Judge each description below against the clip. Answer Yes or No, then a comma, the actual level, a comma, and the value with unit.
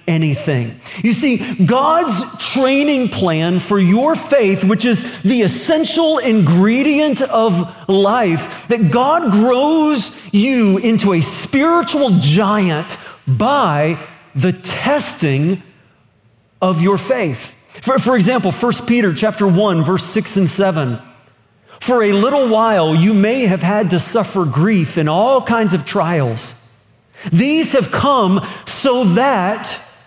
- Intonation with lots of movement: Yes, wide, 6.4 semitones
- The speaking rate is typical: No, slow, 125 wpm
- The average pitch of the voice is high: Yes, high, 195 Hz